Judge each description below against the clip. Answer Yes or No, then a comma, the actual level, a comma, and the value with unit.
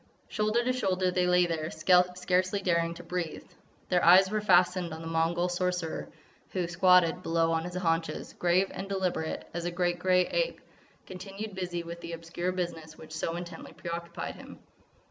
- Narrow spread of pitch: Yes, narrow, 1.6 semitones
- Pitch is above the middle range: No, medium, 180 Hz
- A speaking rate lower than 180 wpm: Yes, average, 170 wpm